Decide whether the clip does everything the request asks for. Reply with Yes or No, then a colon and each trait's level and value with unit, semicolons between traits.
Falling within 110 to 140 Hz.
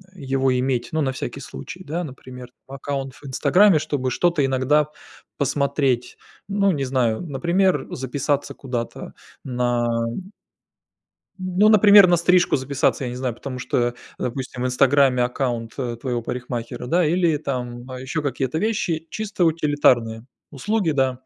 Yes: low, 135 Hz